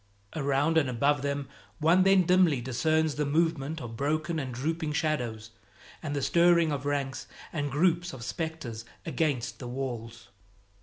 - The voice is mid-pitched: Yes, medium, 145 Hz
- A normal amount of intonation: Yes, average, 3.6 semitones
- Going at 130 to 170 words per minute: Yes, average, 150 wpm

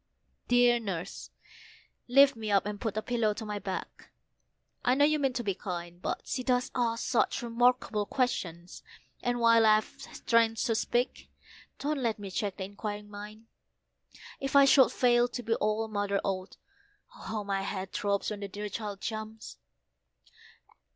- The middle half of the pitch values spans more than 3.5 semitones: No, average, 3.1 semitones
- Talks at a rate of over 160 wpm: Yes, average, 170 wpm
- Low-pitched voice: No, high, 220 Hz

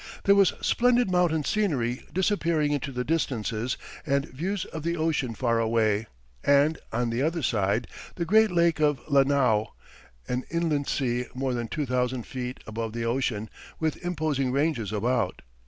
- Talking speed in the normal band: Yes, average, 155 wpm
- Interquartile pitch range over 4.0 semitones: Yes, average, 5.2 semitones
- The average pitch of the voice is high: No, low, 135 Hz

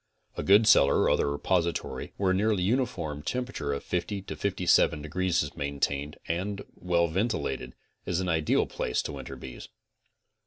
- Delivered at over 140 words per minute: Yes, average, 165 wpm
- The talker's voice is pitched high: No, very low, 85 Hz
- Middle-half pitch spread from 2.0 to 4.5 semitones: No, average, 5.1 semitones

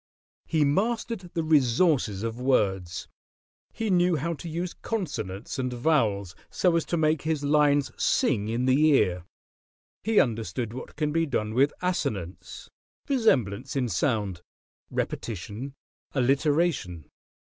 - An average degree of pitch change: No, wide, 6.9 semitones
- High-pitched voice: No, low, 135 Hz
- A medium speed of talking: No, slow, 125 wpm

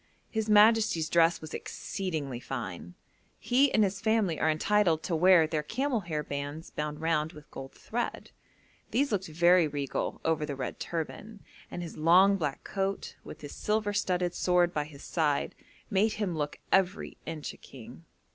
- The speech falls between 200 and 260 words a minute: No, average, 165 wpm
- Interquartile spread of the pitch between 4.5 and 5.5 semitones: Yes, average, 4.8 semitones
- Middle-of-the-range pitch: Yes, medium, 170 Hz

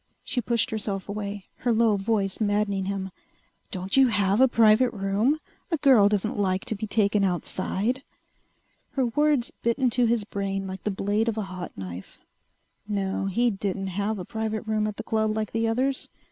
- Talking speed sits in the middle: Yes, average, 180 wpm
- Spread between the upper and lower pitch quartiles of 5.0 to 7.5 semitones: No, average, 2.8 semitones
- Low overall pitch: No, high, 210 Hz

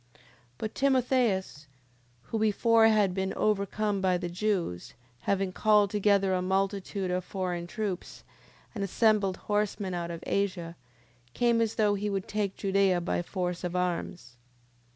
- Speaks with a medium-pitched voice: No, high, 195 Hz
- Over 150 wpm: No, average, 145 wpm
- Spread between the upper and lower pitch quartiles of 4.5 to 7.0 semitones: No, average, 2.7 semitones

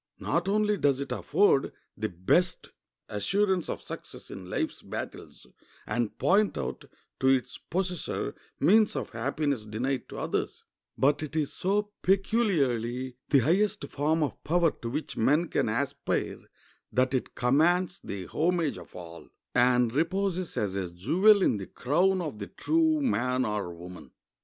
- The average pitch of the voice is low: No, medium, 145 Hz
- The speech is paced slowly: No, average, 150 wpm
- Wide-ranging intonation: Yes, wide, 7.5 semitones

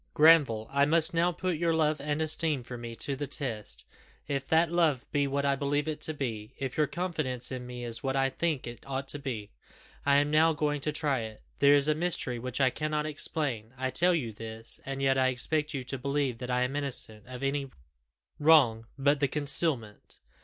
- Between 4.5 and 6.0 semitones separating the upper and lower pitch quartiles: No, average, 3.3 semitones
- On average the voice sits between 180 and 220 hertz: No, medium, 140 Hz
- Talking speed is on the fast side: Yes, fast, 215 wpm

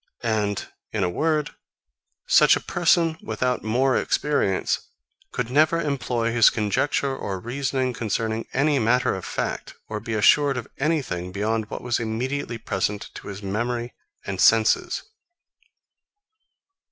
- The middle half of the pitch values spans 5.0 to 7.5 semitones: No, average, 4.3 semitones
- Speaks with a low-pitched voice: Yes, low, 120 Hz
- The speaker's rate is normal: No, slow, 130 wpm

